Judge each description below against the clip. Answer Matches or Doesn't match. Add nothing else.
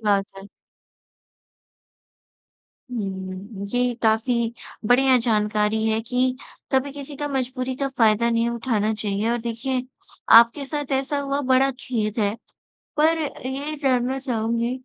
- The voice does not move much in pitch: Doesn't match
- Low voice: Doesn't match